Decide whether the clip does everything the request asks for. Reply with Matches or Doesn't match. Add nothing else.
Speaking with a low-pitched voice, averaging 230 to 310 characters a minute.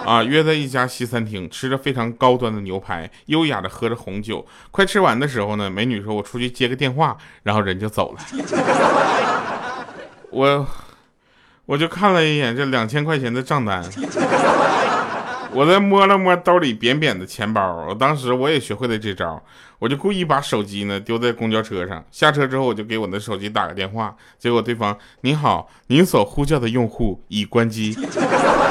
Matches